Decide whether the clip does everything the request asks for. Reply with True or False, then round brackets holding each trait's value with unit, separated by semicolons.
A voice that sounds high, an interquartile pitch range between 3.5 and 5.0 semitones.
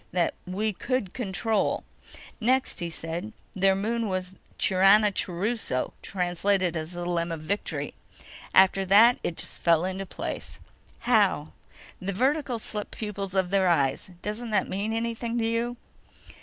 True (195 Hz; 3.8 semitones)